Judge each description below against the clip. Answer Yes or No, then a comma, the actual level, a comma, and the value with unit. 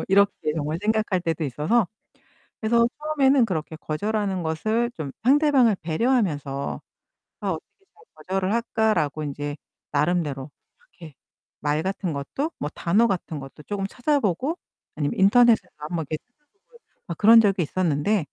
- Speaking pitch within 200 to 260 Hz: No, high, 190 Hz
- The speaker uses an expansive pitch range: Yes, wide, 7.2 semitones